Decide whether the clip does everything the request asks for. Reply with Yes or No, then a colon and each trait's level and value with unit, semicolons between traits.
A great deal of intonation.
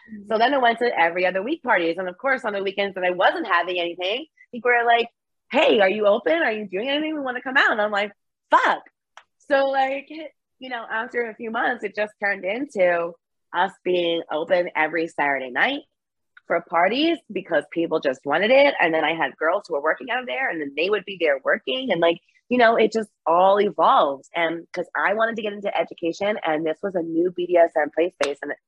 Yes: wide, 5.9 semitones